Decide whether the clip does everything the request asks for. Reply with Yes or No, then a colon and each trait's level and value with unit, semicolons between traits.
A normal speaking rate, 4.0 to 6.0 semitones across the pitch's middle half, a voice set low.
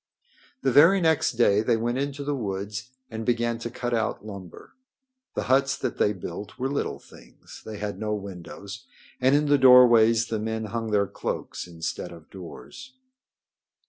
Yes: average, 170 wpm; average, 4.3 semitones; low, 115 Hz